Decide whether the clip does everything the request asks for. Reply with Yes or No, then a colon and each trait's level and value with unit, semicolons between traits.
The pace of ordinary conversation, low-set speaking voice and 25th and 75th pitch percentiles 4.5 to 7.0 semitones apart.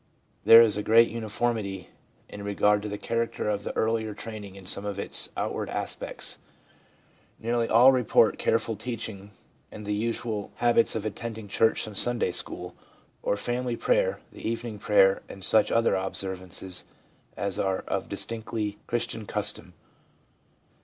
No: average, 145 wpm; low, 110 Hz; narrow, 2.4 semitones